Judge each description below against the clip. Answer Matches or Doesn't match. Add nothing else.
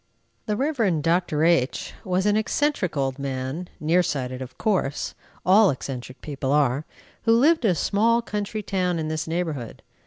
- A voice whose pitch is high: Doesn't match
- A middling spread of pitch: Doesn't match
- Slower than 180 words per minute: Matches